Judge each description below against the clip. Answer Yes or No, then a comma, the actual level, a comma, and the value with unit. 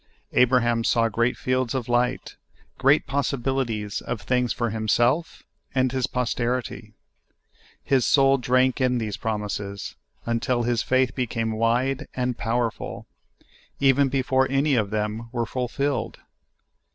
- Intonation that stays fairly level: Yes, narrow, 2.2 semitones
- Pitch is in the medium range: No, low, 125 Hz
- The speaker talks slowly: Yes, slow, 125 wpm